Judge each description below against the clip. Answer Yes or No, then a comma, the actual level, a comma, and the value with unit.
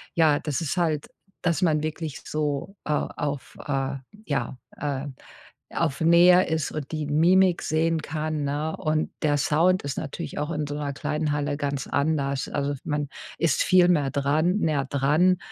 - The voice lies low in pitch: No, medium, 150 Hz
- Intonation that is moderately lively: No, narrow, 2.2 semitones